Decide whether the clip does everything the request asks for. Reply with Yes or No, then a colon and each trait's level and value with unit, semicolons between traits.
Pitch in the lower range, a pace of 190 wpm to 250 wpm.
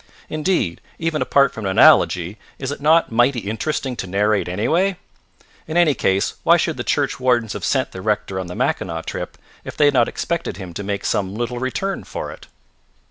Yes: low, 120 Hz; average, 195 wpm